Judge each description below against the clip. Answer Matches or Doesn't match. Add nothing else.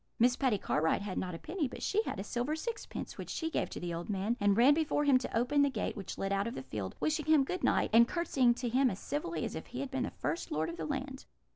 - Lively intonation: Matches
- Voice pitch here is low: Doesn't match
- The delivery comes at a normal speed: Doesn't match